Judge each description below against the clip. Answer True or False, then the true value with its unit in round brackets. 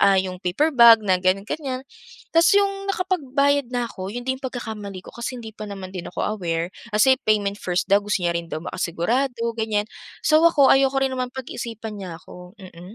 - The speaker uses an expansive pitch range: True (5.9 semitones)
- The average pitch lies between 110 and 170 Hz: False (220 Hz)